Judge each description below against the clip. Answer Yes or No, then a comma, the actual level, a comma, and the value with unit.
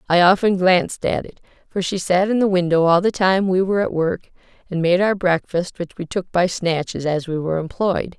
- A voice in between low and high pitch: Yes, medium, 180 Hz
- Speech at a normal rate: No, fast, 225 wpm